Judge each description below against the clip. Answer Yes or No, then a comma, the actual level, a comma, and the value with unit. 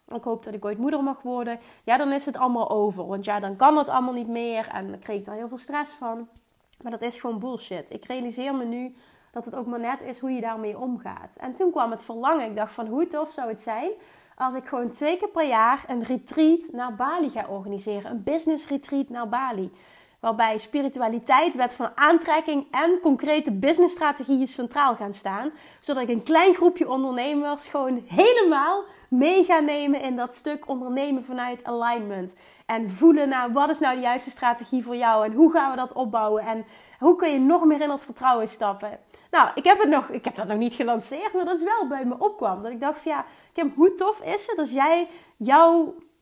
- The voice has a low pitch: No, very high, 255 Hz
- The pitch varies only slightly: No, average, 4.4 semitones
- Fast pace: Yes, fast, 220 wpm